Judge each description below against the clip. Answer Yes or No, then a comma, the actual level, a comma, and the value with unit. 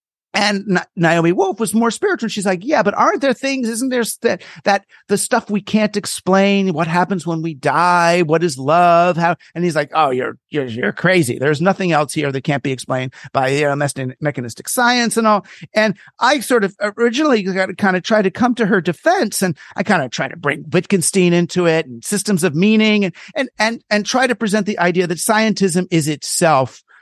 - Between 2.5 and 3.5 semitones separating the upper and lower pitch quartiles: No, average, 4.5 semitones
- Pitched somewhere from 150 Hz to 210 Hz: Yes, high, 190 Hz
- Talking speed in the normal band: No, fast, 215 wpm